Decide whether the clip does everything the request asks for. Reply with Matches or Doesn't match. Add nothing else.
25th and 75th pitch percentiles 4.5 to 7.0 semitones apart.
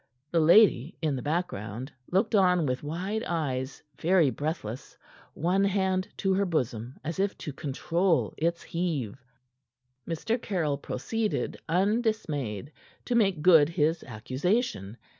Matches